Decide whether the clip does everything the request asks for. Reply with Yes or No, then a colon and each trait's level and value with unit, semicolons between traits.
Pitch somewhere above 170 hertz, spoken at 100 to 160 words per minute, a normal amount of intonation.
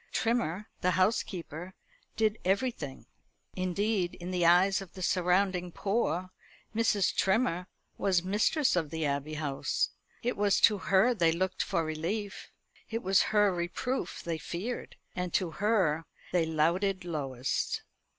Yes: medium, 185 Hz; slow, 135 wpm; average, 3.4 semitones